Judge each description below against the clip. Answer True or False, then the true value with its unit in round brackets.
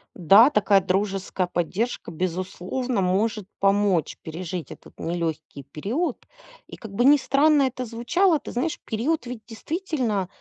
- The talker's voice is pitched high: True (210 Hz)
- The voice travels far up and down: True (5.8 semitones)